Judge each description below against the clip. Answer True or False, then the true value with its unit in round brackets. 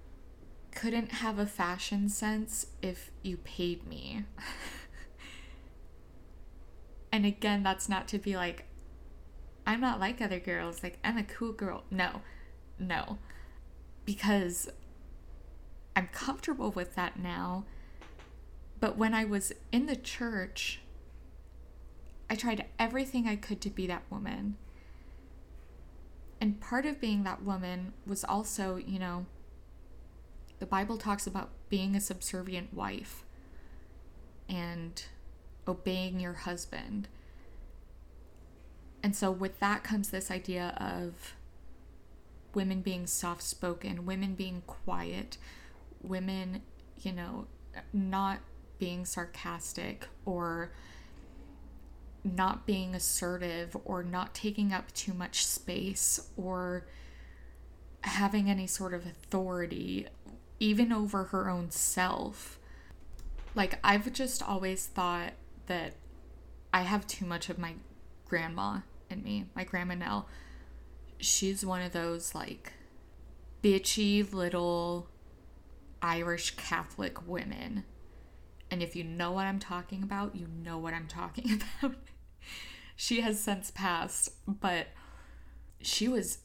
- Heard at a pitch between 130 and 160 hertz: False (180 Hz)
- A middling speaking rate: False (115 wpm)